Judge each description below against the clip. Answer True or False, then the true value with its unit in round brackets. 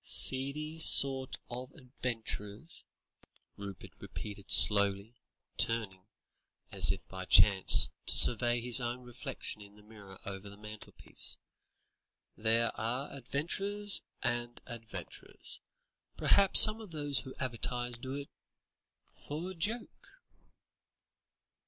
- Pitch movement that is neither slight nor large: True (4.8 semitones)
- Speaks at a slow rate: True (110 wpm)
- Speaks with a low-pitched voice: True (120 Hz)